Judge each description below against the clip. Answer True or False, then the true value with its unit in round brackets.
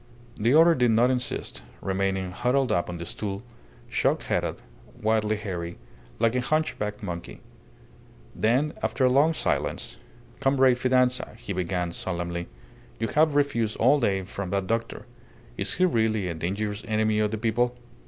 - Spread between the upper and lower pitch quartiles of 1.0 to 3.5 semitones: False (4.7 semitones)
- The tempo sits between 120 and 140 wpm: False (155 wpm)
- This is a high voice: False (110 Hz)